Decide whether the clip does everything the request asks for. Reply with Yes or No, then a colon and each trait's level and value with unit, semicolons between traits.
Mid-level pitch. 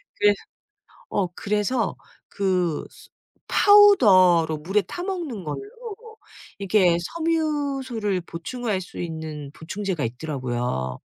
No: high, 200 Hz